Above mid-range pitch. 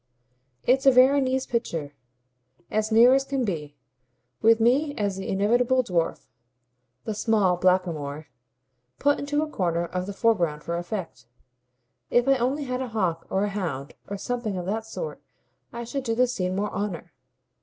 Yes: high, 215 Hz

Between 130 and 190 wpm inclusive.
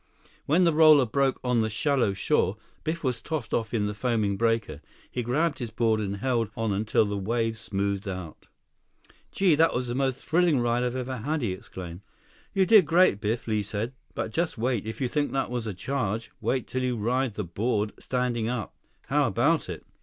No: average, 200 wpm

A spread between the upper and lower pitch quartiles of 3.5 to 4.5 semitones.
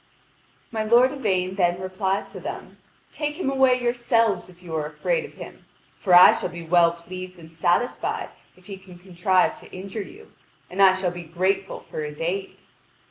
Yes: average, 4.0 semitones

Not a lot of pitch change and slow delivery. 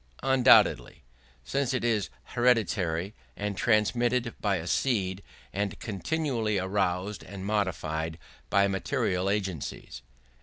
No: average, 4.2 semitones; slow, 105 wpm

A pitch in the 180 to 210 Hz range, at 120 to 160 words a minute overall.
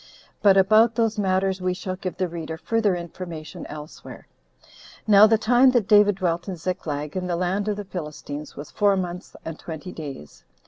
No: medium, 185 Hz; average, 180 wpm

